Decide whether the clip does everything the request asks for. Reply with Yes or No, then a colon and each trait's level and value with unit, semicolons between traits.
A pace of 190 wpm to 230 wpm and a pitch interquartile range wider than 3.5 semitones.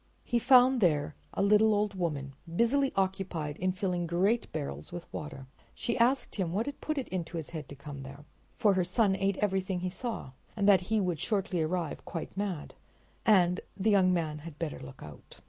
Yes: average, 200 wpm; average, 4.6 semitones